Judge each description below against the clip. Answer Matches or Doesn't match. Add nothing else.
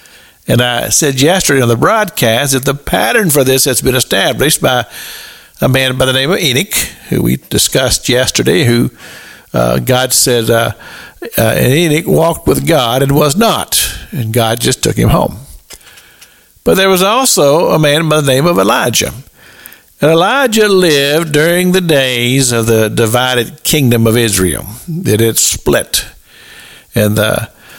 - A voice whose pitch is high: Doesn't match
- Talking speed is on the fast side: Doesn't match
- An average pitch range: Doesn't match